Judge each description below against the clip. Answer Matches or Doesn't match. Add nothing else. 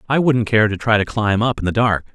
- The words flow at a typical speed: Doesn't match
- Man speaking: Matches